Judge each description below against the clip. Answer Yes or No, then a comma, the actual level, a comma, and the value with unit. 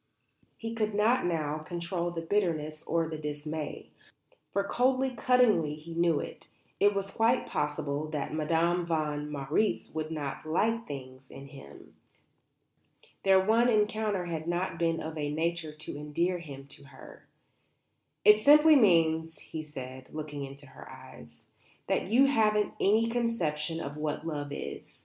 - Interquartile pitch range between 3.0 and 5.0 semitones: No, wide, 5.6 semitones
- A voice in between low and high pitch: Yes, medium, 165 Hz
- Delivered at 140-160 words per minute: Yes, average, 150 wpm